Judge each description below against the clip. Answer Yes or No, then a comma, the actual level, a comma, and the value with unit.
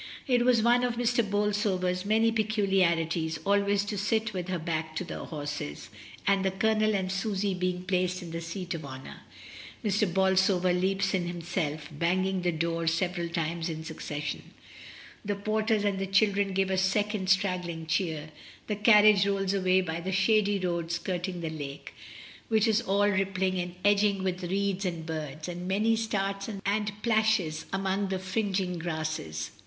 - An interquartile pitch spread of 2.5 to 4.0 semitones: Yes, average, 3.1 semitones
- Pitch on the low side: No, high, 190 Hz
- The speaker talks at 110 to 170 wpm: Yes, average, 165 wpm